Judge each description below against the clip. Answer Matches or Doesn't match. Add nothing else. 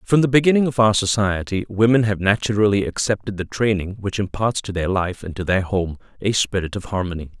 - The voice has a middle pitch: Doesn't match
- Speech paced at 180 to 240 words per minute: Matches